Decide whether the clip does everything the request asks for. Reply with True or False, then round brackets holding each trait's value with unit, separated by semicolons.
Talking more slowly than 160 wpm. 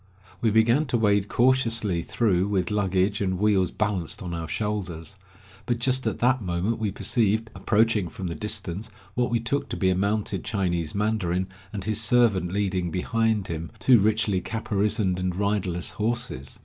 False (165 wpm)